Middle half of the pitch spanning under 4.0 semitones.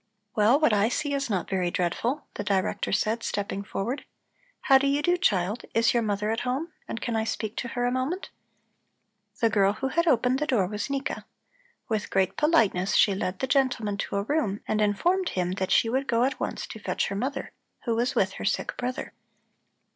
No: average, 4.8 semitones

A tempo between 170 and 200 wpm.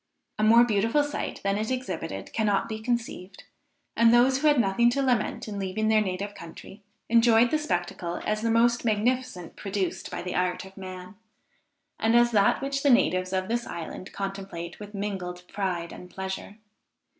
Yes: average, 175 wpm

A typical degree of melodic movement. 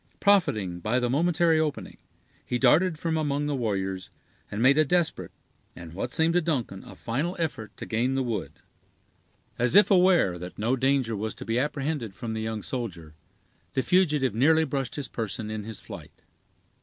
No: wide, 6.2 semitones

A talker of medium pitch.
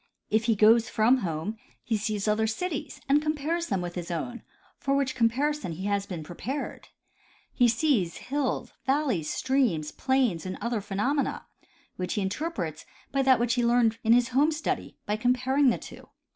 No: high, 235 Hz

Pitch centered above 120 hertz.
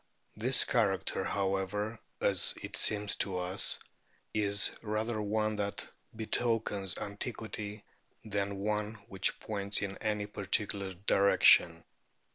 No: low, 105 Hz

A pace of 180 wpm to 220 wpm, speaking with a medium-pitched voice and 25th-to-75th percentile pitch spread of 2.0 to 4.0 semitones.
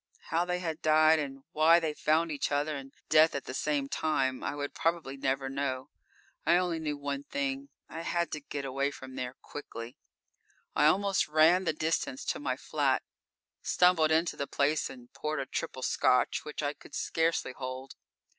Yes: average, 185 wpm; medium, 145 Hz; average, 2.9 semitones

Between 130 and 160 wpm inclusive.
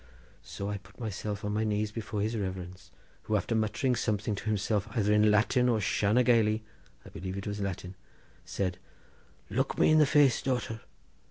No: average, 175 wpm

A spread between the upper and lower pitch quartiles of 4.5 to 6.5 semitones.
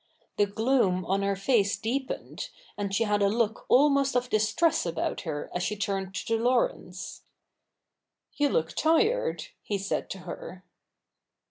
Yes: average, 5.2 semitones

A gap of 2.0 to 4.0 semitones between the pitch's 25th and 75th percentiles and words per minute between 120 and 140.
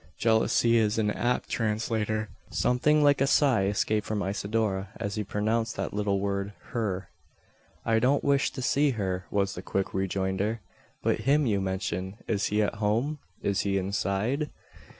No: average, 2.9 semitones; average, 160 wpm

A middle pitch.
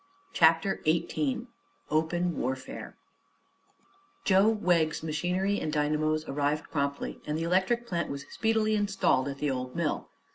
Yes: medium, 165 Hz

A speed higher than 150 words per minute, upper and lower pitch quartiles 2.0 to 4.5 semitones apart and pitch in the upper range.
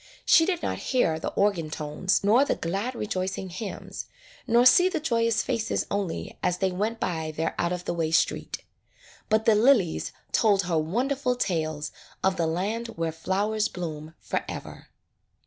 No: average, 165 wpm; wide, 5.6 semitones; high, 195 Hz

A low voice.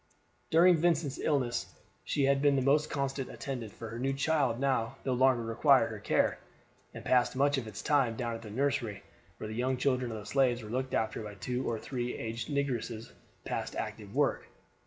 Yes: low, 130 Hz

